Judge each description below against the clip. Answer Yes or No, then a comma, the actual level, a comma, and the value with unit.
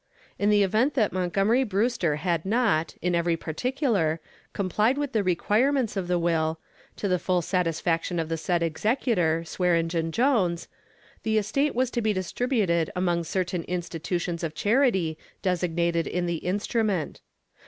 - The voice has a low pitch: No, medium, 180 Hz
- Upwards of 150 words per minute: No, average, 145 wpm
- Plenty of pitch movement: No, average, 4.5 semitones